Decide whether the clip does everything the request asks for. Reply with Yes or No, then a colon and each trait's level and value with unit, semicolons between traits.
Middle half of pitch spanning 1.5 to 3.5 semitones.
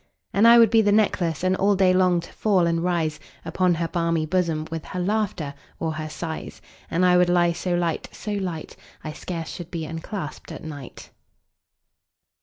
Yes: narrow, 2.4 semitones